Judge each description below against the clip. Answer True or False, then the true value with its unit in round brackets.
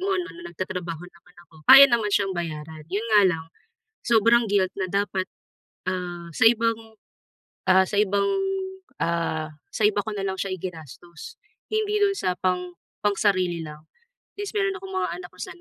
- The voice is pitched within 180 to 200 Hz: True (190 Hz)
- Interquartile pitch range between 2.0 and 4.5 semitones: False (4.9 semitones)